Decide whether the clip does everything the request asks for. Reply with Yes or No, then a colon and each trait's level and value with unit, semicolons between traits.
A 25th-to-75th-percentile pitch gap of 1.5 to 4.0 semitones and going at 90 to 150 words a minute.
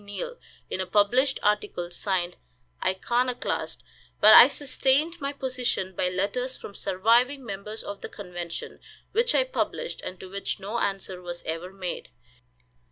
No: wide, 5.6 semitones; average, 145 wpm